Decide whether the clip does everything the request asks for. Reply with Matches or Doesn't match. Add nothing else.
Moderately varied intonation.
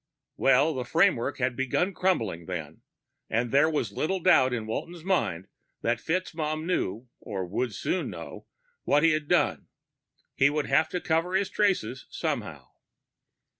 Doesn't match